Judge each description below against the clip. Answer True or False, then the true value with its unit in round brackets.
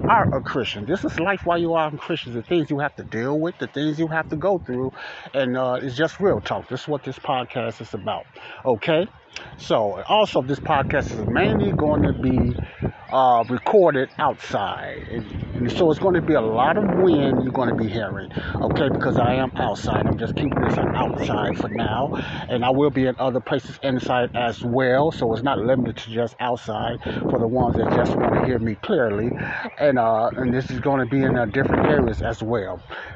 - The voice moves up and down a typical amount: True (3.7 semitones)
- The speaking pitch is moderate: False (130 Hz)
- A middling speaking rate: False (215 wpm)